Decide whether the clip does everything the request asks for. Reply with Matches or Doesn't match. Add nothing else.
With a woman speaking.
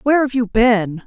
Matches